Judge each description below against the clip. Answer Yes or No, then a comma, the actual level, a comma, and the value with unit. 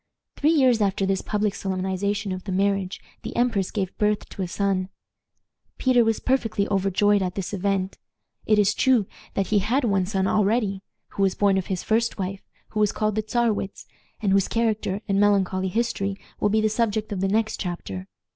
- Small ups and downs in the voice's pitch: Yes, narrow, 2.1 semitones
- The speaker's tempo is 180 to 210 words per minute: Yes, average, 190 wpm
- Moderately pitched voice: No, high, 200 Hz